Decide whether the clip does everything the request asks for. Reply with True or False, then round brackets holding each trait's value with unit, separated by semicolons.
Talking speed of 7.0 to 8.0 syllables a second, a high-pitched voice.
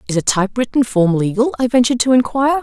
True (7.1 syllables/s; 235 Hz)